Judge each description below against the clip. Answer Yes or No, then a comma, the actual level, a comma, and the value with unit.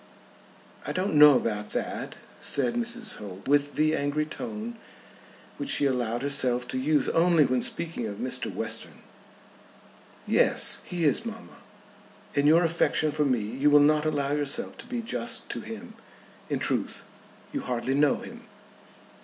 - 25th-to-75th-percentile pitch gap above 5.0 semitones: Yes, wide, 5.4 semitones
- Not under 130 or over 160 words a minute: Yes, average, 155 wpm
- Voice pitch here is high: No, medium, 150 Hz